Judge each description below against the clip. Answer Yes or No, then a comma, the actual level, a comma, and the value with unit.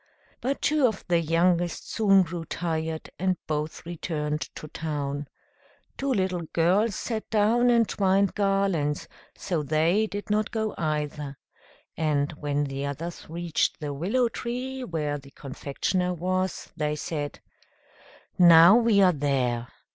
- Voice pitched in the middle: Yes, medium, 170 Hz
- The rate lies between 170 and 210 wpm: No, slow, 135 wpm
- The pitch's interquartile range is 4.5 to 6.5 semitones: Yes, average, 5.0 semitones